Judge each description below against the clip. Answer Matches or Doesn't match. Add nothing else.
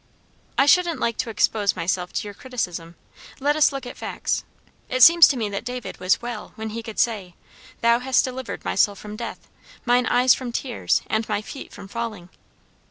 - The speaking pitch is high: Matches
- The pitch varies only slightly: Doesn't match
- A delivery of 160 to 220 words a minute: Matches